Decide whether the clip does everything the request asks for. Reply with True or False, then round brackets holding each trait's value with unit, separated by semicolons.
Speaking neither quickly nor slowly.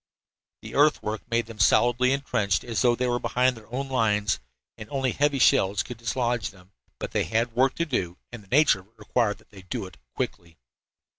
False (210 wpm)